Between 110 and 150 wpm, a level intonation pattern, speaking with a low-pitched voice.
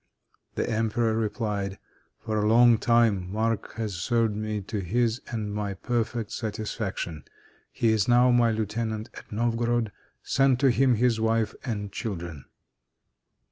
Yes: average, 140 wpm; narrow, 2.2 semitones; low, 110 Hz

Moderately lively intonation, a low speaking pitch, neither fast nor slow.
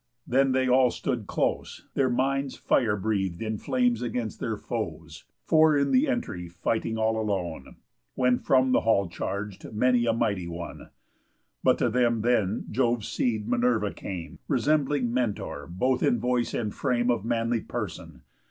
Yes: average, 3.3 semitones; low, 120 Hz; average, 155 wpm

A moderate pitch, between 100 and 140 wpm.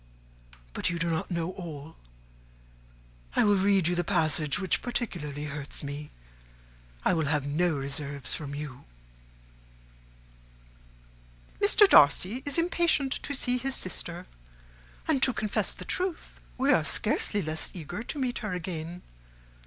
Yes: medium, 175 Hz; slow, 135 wpm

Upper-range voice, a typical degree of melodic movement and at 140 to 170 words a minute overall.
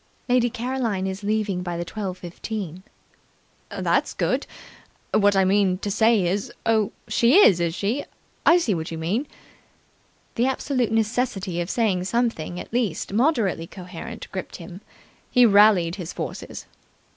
Yes: high, 200 Hz; average, 4.3 semitones; average, 145 wpm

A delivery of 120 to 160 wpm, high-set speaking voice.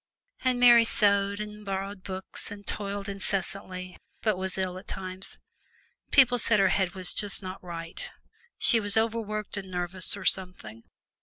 Yes: average, 155 wpm; high, 195 Hz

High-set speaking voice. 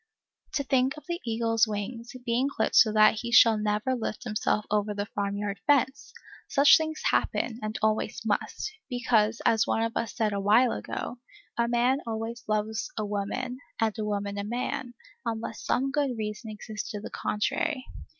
Yes: high, 225 Hz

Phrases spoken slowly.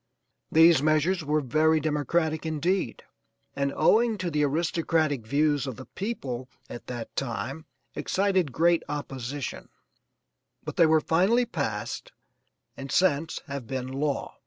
Yes: slow, 130 wpm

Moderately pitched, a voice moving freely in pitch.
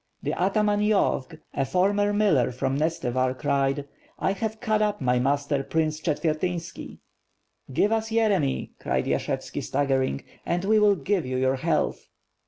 Yes: medium, 160 Hz; wide, 7.2 semitones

